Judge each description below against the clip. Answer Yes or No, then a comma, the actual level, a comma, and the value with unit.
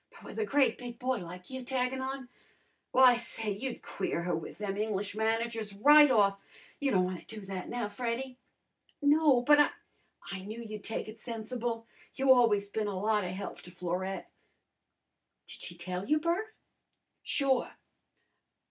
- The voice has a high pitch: Yes, high, 225 Hz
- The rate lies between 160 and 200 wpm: Yes, average, 170 wpm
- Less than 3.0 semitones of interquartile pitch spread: No, average, 4.7 semitones